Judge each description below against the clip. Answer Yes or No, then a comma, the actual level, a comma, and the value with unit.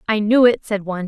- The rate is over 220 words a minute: Yes, fast, 280 wpm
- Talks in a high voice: Yes, high, 210 Hz